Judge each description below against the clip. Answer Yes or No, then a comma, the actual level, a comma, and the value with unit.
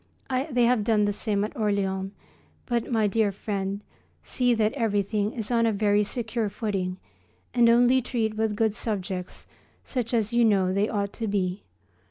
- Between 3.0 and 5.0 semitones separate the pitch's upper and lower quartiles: No, narrow, 2.5 semitones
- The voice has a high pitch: Yes, high, 215 Hz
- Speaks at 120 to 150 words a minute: No, average, 170 wpm